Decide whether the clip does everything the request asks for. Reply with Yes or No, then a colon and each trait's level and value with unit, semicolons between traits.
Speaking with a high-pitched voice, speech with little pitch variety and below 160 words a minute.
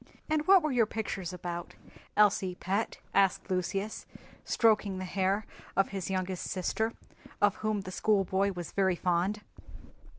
Yes: high, 195 Hz; narrow, 2.3 semitones; average, 140 wpm